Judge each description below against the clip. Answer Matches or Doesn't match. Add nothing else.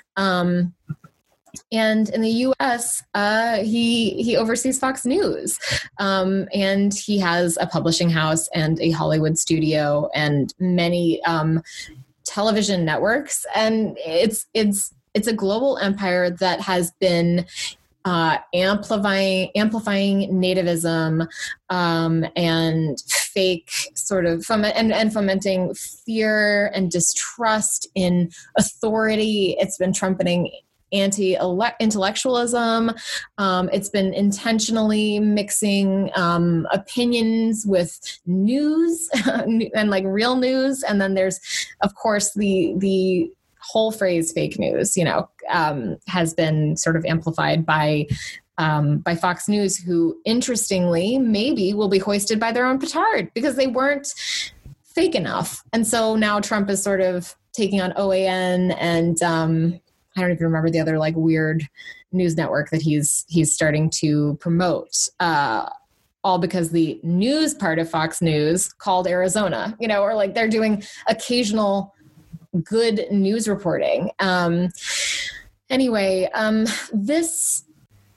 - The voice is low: Doesn't match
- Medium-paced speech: Doesn't match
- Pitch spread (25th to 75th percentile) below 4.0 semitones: Doesn't match